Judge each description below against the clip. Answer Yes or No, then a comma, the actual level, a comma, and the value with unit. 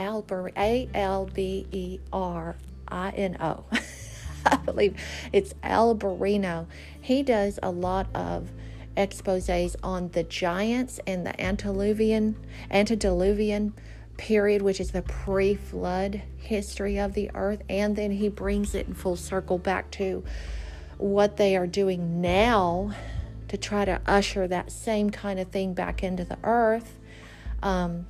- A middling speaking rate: No, slow, 125 wpm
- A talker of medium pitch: No, high, 195 Hz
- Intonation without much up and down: Yes, narrow, 2.2 semitones